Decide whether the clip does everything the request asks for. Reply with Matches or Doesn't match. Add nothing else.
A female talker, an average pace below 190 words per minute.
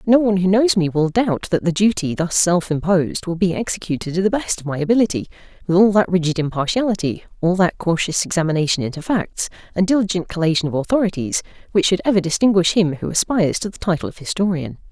Doesn't match